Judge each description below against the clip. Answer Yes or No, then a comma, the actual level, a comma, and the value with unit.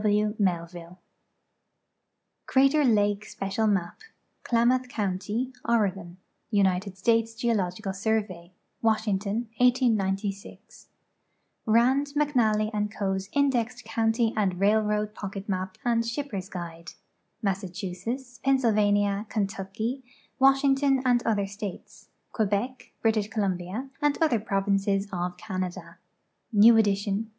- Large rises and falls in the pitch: No, average, 3.2 semitones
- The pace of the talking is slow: Yes, slow, 105 wpm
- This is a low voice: No, high, 210 Hz